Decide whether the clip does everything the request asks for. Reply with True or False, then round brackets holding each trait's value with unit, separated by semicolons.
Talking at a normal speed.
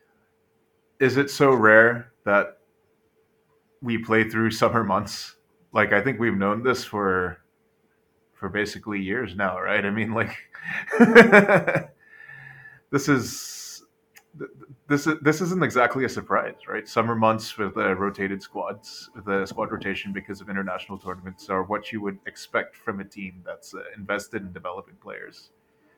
True (145 wpm)